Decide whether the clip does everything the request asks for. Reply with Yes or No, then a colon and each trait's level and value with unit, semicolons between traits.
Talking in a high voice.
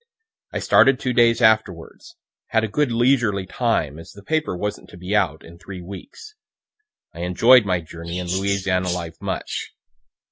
No: low, 100 Hz